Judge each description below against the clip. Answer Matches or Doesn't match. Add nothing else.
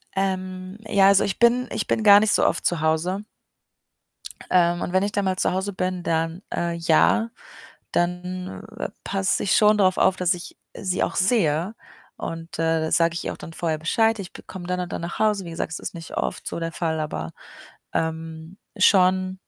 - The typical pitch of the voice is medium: Matches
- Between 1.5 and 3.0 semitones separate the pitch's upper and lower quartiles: Matches